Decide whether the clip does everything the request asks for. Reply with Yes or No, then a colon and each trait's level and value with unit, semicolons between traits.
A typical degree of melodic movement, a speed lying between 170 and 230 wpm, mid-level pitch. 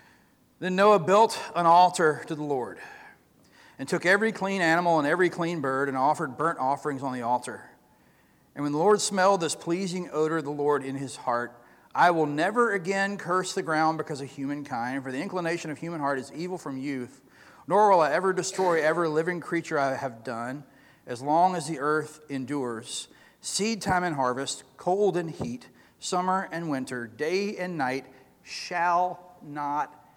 Yes: average, 4.7 semitones; average, 180 wpm; medium, 155 Hz